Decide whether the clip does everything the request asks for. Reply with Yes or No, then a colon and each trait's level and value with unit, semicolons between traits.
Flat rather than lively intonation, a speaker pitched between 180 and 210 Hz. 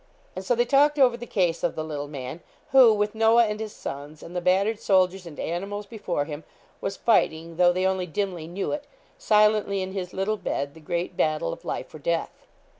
No: average, 4.4 semitones; high, 190 Hz